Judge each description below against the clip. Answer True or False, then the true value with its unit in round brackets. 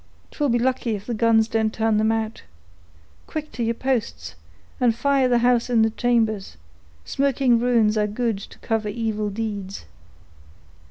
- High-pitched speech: True (225 Hz)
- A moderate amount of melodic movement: False (2.2 semitones)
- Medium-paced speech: True (160 wpm)